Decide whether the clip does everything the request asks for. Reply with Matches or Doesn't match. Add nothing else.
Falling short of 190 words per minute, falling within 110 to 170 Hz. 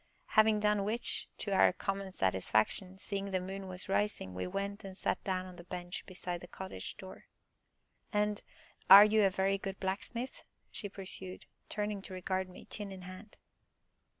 Doesn't match